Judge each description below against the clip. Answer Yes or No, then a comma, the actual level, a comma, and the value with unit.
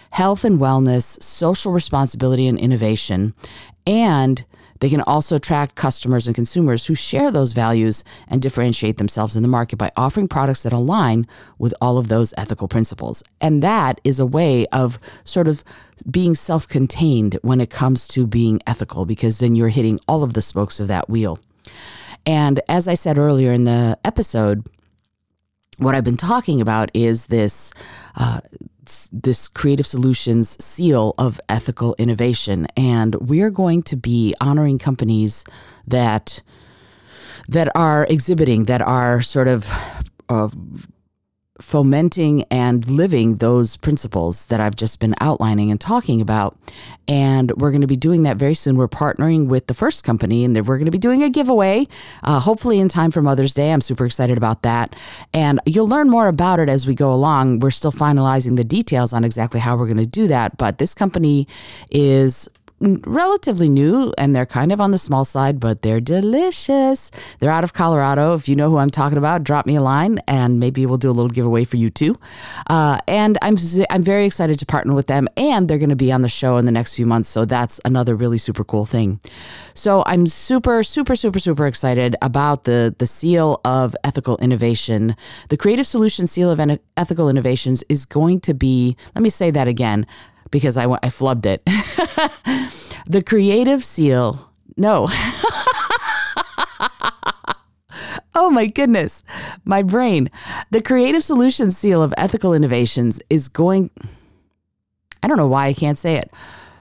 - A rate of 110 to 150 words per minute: No, average, 175 wpm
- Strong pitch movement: Yes, wide, 5.9 semitones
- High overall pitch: No, low, 135 Hz